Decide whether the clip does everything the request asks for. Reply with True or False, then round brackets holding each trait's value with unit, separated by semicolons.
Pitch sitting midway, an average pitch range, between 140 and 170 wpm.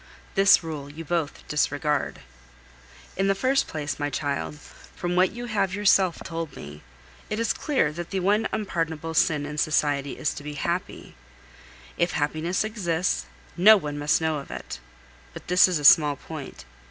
True (165 Hz; 4.3 semitones; 165 wpm)